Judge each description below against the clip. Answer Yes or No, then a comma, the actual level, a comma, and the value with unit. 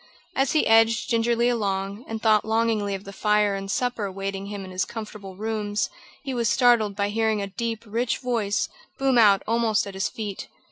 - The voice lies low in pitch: No, high, 215 Hz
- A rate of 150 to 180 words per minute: No, average, 190 wpm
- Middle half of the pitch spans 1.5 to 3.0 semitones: Yes, narrow, 2.5 semitones